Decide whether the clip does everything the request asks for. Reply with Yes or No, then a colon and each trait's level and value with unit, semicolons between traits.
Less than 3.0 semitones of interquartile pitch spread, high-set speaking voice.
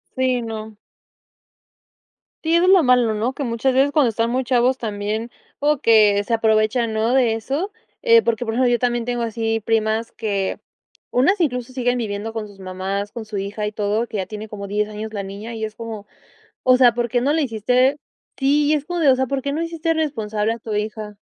No: average, 3.3 semitones; high, 230 Hz